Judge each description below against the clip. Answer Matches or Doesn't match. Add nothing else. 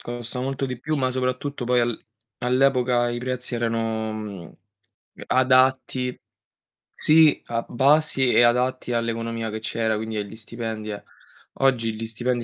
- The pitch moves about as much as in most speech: Doesn't match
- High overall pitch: Doesn't match